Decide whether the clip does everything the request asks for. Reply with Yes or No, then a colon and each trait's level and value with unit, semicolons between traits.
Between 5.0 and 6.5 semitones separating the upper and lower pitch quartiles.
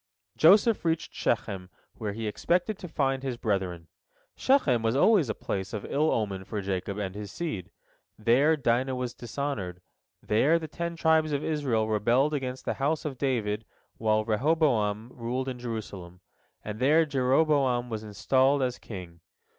Yes: wide, 5.6 semitones